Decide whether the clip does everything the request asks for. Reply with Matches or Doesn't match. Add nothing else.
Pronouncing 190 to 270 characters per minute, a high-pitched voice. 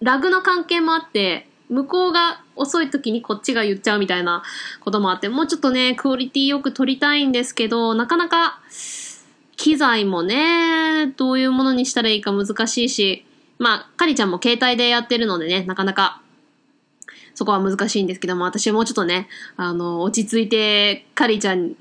Doesn't match